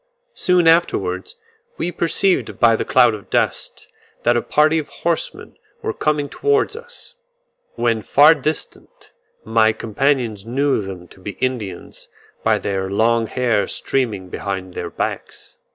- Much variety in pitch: Yes, wide, 6.7 semitones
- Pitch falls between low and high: No, low, 120 Hz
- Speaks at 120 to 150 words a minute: Yes, slow, 135 wpm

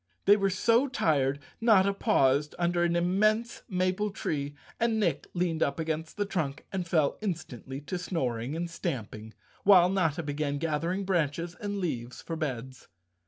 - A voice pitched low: No, medium, 170 Hz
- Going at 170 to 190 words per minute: No, average, 155 wpm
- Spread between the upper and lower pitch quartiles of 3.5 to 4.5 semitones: No, average, 5.1 semitones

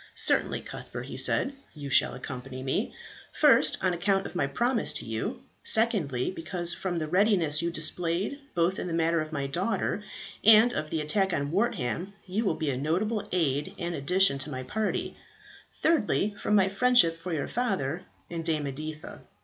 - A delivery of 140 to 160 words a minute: No, average, 175 wpm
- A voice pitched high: No, medium, 170 Hz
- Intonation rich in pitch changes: No, average, 5.0 semitones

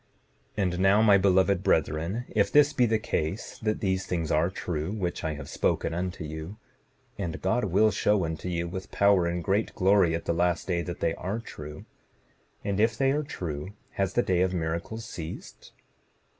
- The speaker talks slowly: No, average, 190 wpm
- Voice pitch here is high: No, very low, 95 Hz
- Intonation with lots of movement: No, average, 3.5 semitones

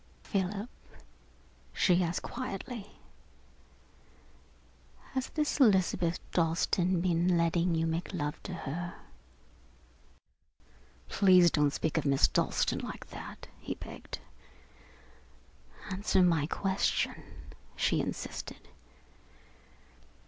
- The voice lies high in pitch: No, medium, 180 Hz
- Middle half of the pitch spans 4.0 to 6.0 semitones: No, average, 2.7 semitones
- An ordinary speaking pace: No, slow, 90 wpm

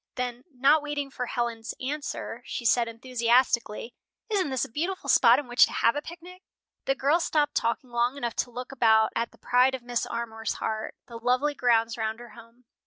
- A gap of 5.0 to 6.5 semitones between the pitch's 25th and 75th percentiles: No, average, 3.0 semitones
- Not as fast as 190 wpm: No, average, 195 wpm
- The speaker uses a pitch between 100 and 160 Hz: No, high, 245 Hz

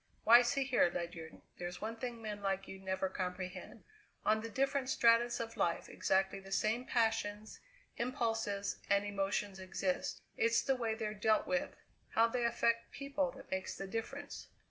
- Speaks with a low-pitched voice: No, high, 220 Hz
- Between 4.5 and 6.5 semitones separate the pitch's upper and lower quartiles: No, average, 3.6 semitones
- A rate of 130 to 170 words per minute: Yes, average, 165 wpm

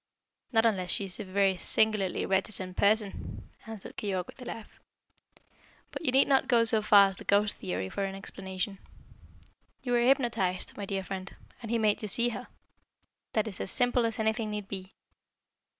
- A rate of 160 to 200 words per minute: Yes, average, 180 wpm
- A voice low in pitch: No, high, 210 Hz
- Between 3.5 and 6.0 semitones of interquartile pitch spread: No, average, 3.0 semitones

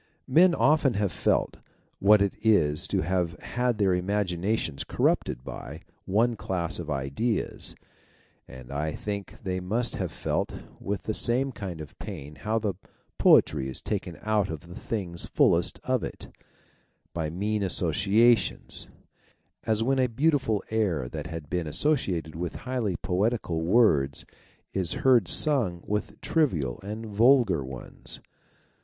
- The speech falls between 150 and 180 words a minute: No, average, 140 wpm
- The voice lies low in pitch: Yes, low, 100 Hz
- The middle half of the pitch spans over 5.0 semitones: Yes, wide, 5.4 semitones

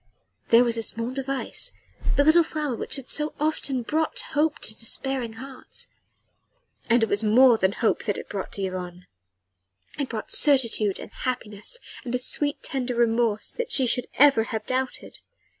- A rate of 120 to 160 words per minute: No, average, 175 wpm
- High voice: Yes, high, 245 Hz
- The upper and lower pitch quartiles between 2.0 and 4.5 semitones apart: Yes, average, 3.7 semitones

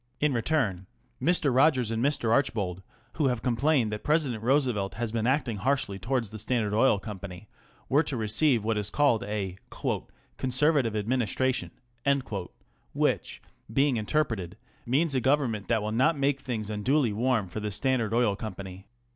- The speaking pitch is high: No, low, 120 Hz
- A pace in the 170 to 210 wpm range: No, average, 160 wpm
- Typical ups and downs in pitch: Yes, average, 4.3 semitones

